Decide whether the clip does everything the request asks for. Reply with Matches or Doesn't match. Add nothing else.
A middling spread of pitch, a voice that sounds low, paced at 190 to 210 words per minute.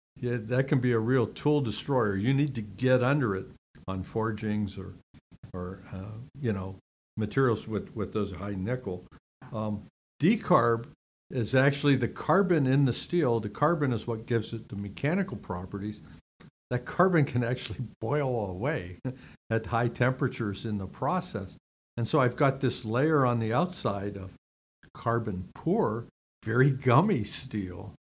Doesn't match